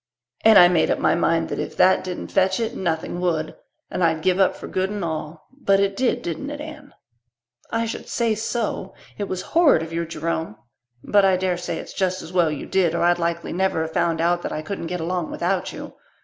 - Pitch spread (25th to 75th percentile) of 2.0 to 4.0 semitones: Yes, average, 2.9 semitones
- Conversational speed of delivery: No, fast, 225 wpm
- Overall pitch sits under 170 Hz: No, medium, 180 Hz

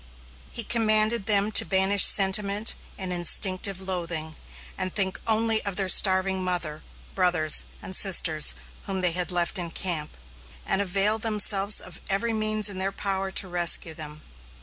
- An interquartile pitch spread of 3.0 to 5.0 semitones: No, narrow, 2.5 semitones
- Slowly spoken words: No, average, 150 wpm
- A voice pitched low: No, high, 190 Hz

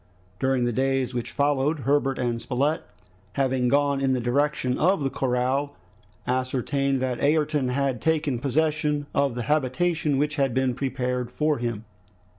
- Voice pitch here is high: No, low, 135 Hz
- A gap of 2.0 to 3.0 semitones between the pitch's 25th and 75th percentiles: Yes, narrow, 2.4 semitones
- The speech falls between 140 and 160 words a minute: Yes, average, 150 wpm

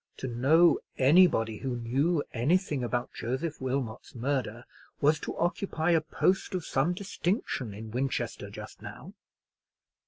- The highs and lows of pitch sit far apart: Yes, wide, 5.7 semitones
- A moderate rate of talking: No, slow, 130 wpm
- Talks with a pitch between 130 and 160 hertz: Yes, low, 135 Hz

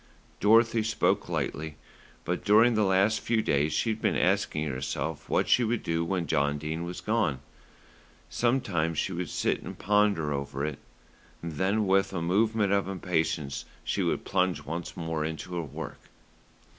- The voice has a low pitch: Yes, very low, 90 Hz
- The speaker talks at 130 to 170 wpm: Yes, average, 160 wpm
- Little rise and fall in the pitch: No, average, 5.2 semitones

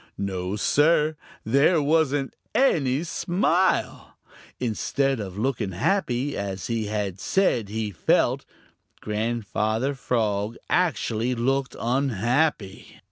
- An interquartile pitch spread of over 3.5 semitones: Yes, wide, 5.4 semitones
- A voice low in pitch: Yes, low, 125 Hz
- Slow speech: Yes, slow, 90 wpm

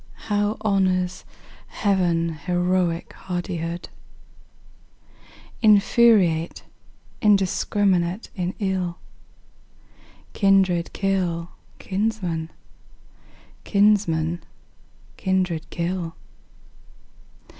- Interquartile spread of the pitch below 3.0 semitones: Yes, narrow, 2.6 semitones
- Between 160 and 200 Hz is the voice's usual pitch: Yes, medium, 185 Hz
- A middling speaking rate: No, slow, 50 wpm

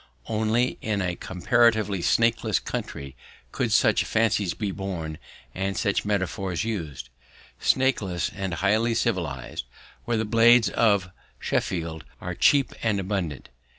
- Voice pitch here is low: Yes, low, 100 Hz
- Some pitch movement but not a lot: Yes, average, 4.1 semitones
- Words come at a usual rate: No, slow, 120 wpm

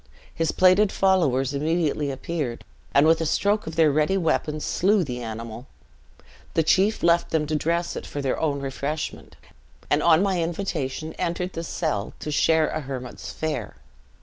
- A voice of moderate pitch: Yes, medium, 155 Hz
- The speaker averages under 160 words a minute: No, average, 165 wpm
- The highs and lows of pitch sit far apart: No, average, 3.4 semitones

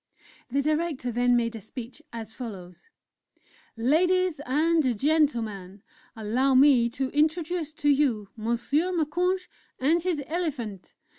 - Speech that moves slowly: Yes, slow, 120 wpm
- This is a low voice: No, very high, 275 Hz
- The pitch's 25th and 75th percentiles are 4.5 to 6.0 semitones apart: Yes, wide, 5.5 semitones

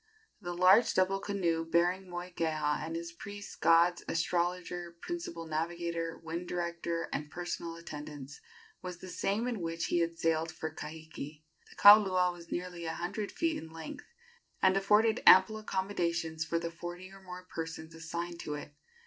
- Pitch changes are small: Yes, narrow, 2.0 semitones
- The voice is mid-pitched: Yes, medium, 170 Hz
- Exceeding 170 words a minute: No, average, 155 wpm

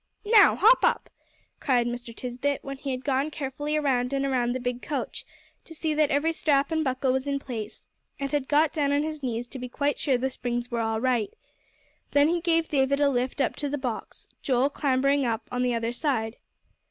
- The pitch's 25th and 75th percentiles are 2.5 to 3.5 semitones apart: Yes, average, 2.8 semitones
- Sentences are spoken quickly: Yes, fast, 215 wpm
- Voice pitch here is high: Yes, very high, 270 Hz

